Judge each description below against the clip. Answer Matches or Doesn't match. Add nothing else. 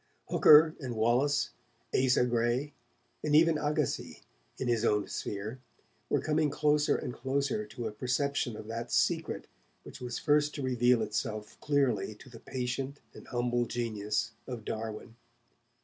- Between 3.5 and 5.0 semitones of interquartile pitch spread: Matches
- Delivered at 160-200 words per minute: Doesn't match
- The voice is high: Doesn't match